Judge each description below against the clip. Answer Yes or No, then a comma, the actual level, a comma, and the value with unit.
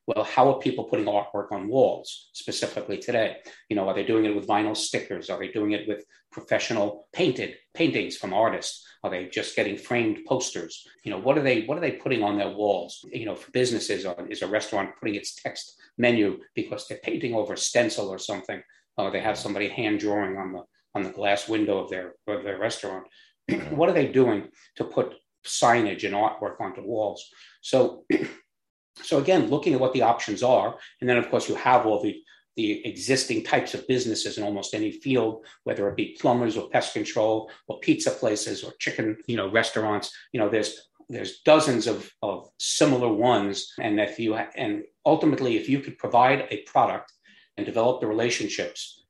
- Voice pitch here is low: Yes, low, 110 Hz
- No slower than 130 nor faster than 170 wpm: No, average, 195 wpm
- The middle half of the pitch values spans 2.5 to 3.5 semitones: No, average, 4.6 semitones